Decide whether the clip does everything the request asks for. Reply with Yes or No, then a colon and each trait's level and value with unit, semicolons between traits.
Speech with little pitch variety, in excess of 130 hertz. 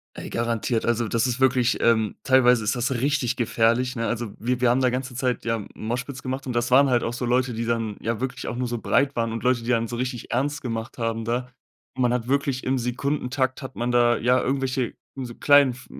No: narrow, 1.8 semitones; low, 125 Hz